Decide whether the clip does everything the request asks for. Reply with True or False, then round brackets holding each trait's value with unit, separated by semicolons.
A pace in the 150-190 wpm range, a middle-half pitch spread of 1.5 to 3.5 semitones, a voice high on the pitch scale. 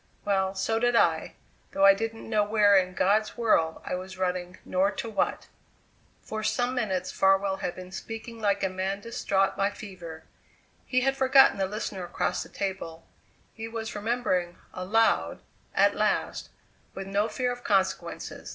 True (160 wpm; 3.2 semitones; 200 Hz)